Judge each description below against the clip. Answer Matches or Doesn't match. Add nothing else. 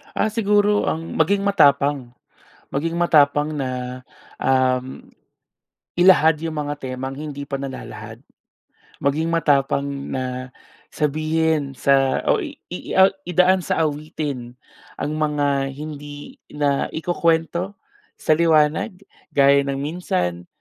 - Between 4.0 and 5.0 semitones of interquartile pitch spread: Doesn't match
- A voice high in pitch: Doesn't match